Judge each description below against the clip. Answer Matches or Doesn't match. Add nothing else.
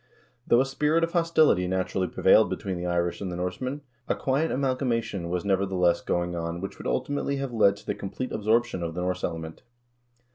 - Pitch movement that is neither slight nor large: Doesn't match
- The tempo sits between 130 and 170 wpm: Doesn't match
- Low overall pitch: Matches